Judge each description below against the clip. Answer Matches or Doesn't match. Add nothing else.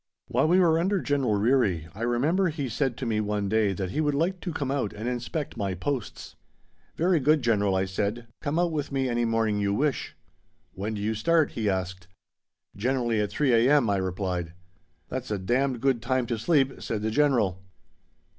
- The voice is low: Matches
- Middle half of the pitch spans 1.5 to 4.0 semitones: Doesn't match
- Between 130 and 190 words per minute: Doesn't match